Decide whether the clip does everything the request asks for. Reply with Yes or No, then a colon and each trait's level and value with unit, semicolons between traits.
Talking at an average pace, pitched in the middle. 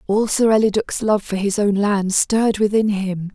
No: average, 195 wpm; high, 205 Hz